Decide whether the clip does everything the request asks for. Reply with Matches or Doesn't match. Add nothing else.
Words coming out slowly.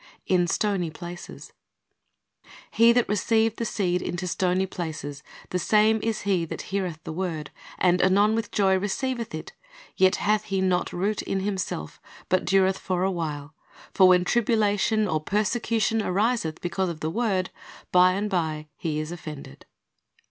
Doesn't match